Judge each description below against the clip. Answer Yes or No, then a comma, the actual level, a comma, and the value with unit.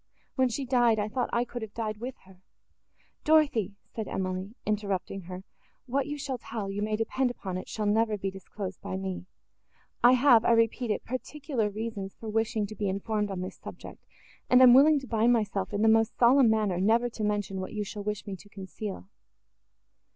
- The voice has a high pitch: Yes, high, 215 Hz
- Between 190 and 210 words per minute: Yes, average, 200 wpm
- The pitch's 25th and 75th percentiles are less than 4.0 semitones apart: Yes, average, 3.4 semitones